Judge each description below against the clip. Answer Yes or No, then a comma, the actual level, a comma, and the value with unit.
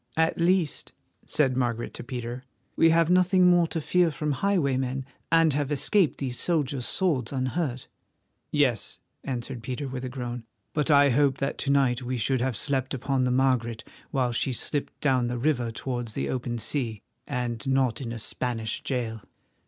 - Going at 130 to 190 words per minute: Yes, average, 170 wpm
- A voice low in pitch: Yes, low, 130 Hz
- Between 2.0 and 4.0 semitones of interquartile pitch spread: Yes, average, 3.2 semitones